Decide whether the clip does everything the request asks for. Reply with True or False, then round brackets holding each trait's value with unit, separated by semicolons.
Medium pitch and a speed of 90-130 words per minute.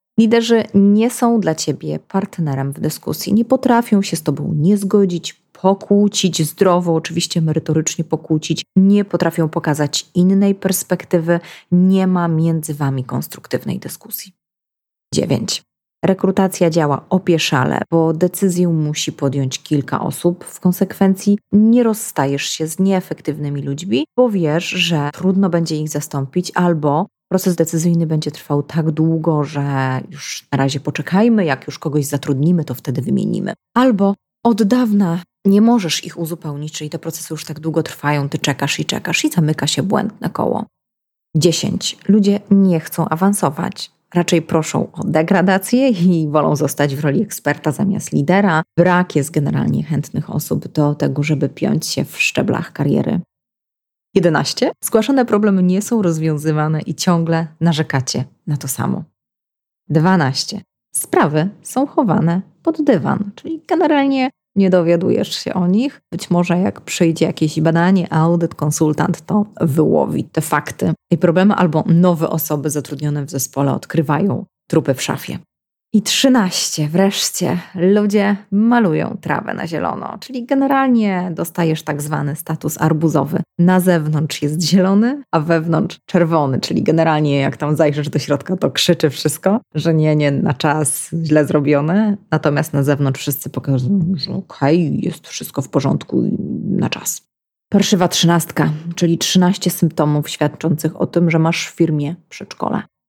False (170 Hz; 140 wpm)